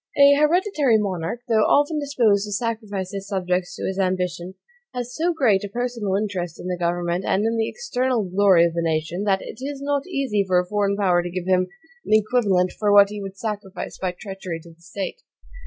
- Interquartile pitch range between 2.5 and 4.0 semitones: No, average, 4.7 semitones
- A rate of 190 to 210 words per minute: Yes, fast, 205 wpm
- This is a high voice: Yes, high, 200 Hz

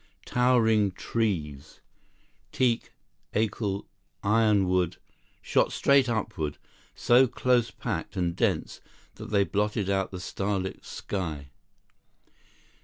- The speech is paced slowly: Yes, slow, 95 wpm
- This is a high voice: No, low, 100 Hz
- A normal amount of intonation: Yes, average, 3.7 semitones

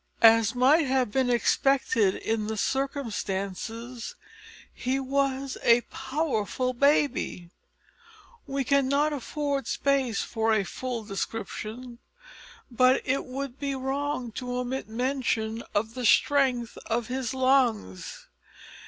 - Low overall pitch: No, very high, 255 Hz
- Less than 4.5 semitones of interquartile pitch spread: Yes, average, 3.2 semitones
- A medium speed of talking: No, slow, 110 wpm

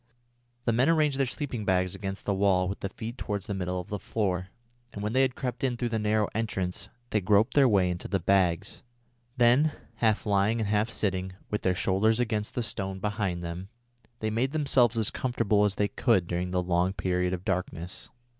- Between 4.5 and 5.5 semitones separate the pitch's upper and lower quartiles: No, average, 3.8 semitones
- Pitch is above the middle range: No, low, 105 Hz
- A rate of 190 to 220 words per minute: Yes, fast, 205 wpm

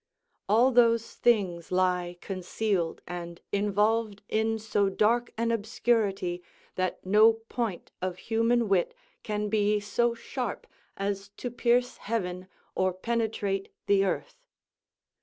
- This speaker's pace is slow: Yes, slow, 120 wpm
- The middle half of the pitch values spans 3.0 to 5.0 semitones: Yes, average, 3.5 semitones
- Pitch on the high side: Yes, high, 210 Hz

